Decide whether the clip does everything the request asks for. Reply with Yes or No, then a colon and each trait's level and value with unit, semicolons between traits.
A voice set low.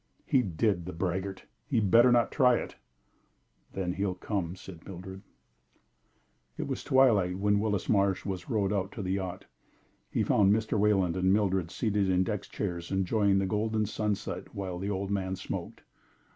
Yes: low, 100 Hz